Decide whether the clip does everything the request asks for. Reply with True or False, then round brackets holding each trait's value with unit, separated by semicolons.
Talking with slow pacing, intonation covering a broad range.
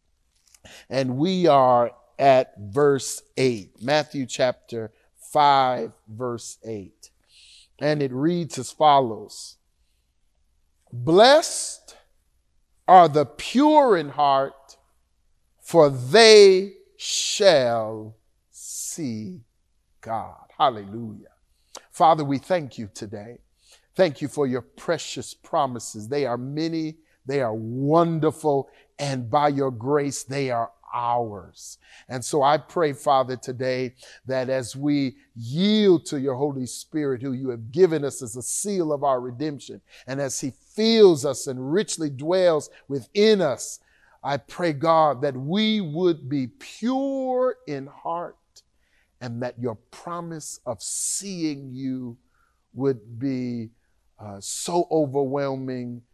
False (115 wpm; 4.7 semitones)